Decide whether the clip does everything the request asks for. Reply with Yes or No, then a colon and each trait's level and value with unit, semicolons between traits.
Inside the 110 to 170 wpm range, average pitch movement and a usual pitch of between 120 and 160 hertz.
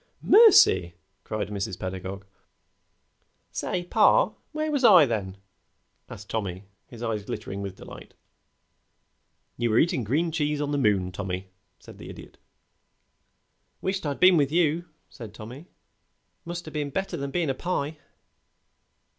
No: average, 140 wpm; wide, 9.0 semitones; low, 135 Hz